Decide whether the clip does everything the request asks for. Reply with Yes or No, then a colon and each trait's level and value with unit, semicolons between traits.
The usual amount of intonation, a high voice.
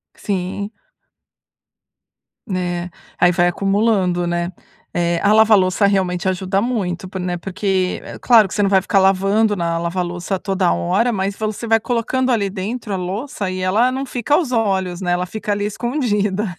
Yes: average, 3.1 semitones; high, 195 Hz